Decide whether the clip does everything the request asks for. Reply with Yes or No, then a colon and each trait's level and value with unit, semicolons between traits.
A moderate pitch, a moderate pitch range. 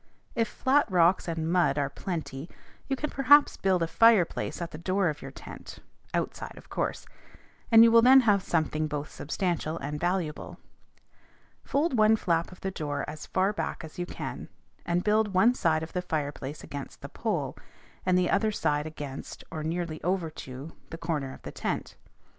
Yes: medium, 175 Hz; average, 4.7 semitones